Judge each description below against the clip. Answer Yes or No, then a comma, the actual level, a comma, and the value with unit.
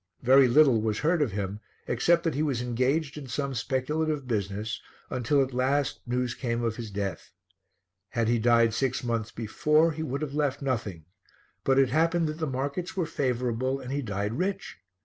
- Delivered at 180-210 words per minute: Yes, average, 185 wpm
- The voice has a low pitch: Yes, low, 130 Hz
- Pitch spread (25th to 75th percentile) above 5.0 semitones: No, average, 4.2 semitones